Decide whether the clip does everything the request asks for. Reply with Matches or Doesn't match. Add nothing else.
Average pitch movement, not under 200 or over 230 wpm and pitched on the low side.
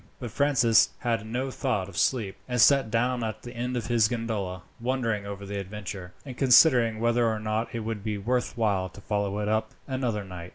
Matches